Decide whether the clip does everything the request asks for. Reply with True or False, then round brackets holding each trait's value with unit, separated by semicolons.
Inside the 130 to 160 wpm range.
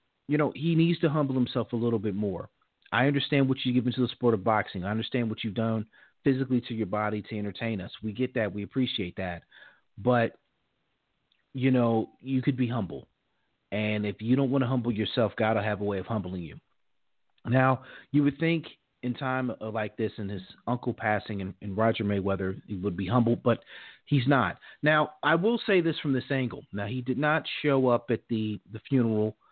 False (205 wpm)